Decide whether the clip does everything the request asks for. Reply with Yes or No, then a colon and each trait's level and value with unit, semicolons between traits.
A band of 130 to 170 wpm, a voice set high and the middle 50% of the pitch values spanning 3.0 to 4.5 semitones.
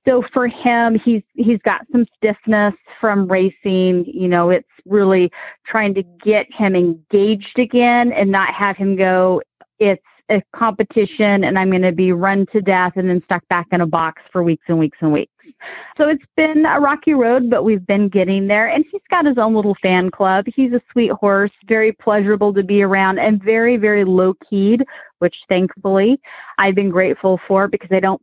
No: average, 195 wpm; high, 205 Hz; average, 3.7 semitones